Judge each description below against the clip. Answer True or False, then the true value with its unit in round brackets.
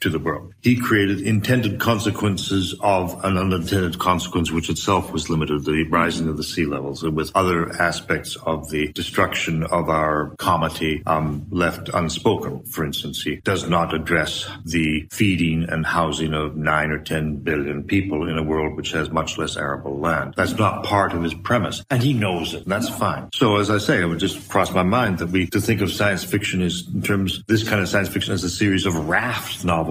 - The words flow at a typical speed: False (210 wpm)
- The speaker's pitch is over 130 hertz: False (90 Hz)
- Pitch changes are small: False (3.6 semitones)